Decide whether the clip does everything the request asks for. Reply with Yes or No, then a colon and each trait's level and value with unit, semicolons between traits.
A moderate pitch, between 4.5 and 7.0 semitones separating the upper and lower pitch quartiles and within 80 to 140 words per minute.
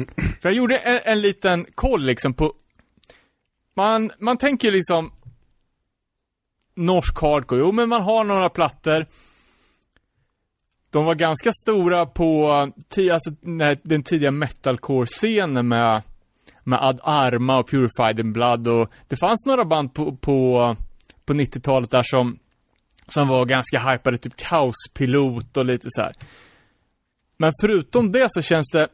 Yes: medium, 150 Hz; wide, 5.6 semitones; average, 135 wpm